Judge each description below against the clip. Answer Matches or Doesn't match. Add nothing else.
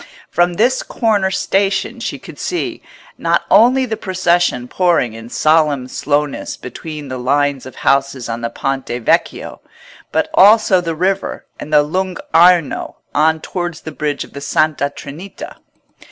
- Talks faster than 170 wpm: Doesn't match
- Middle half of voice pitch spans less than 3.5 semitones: Doesn't match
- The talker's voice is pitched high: Doesn't match